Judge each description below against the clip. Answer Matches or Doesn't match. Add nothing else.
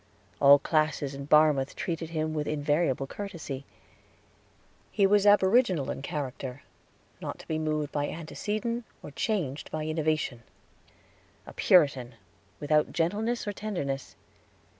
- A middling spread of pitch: Matches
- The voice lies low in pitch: Doesn't match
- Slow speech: Matches